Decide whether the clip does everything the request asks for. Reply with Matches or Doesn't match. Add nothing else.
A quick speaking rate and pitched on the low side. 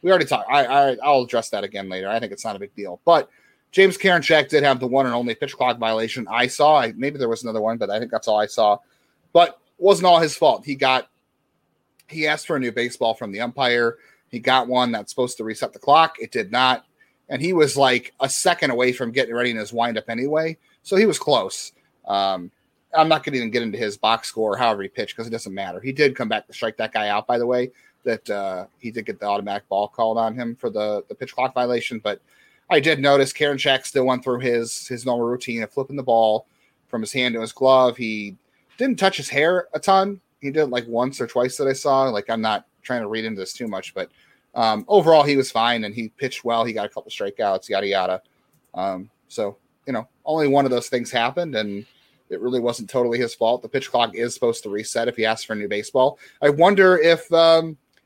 Matches